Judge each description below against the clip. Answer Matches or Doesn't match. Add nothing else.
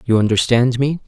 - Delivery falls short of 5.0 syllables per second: Doesn't match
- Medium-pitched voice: Doesn't match